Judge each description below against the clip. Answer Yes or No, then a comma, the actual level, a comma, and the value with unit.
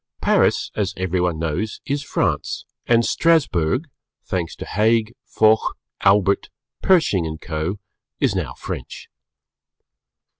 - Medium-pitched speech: No, low, 100 Hz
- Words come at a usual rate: No, slow, 110 wpm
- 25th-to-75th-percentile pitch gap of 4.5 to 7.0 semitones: Yes, average, 5.3 semitones